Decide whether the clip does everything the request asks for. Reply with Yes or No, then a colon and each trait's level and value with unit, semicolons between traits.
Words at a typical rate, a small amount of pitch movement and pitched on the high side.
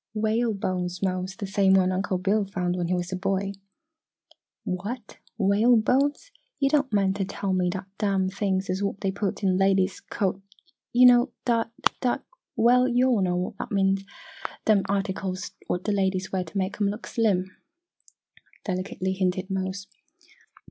Yes: average, 165 wpm; narrow, 2.2 semitones; high, 195 Hz